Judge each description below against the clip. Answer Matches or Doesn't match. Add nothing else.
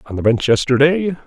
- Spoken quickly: Doesn't match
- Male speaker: Matches